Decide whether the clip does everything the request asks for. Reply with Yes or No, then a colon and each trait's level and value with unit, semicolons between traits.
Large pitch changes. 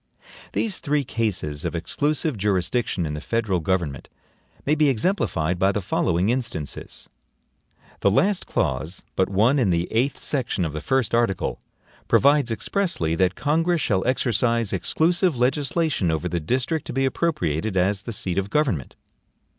Yes: wide, 7.8 semitones